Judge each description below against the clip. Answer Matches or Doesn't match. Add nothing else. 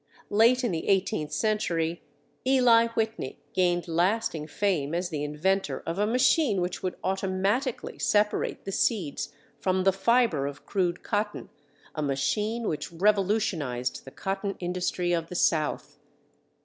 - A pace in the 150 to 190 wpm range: Doesn't match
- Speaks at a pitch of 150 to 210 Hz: Matches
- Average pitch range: Matches